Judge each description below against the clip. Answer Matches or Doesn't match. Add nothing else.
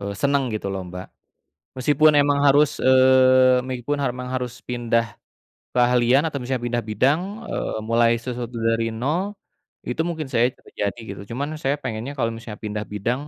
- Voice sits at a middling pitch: Doesn't match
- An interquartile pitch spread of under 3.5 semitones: Matches